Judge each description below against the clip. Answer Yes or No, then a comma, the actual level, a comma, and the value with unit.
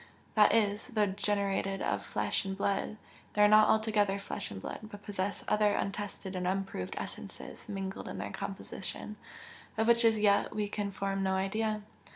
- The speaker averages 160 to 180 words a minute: Yes, average, 175 wpm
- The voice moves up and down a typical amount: No, narrow, 1.6 semitones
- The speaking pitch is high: Yes, high, 205 Hz